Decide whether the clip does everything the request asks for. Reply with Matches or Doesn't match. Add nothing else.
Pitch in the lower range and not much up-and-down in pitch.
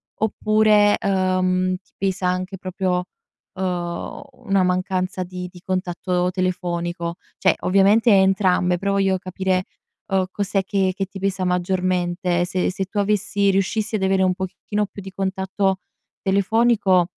Doesn't match